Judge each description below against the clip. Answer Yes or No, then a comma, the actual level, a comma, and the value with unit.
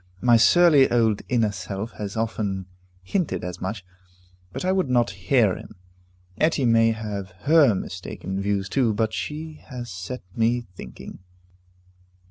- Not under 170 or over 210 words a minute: No, average, 140 wpm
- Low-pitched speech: Yes, low, 115 Hz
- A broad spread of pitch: No, average, 4.4 semitones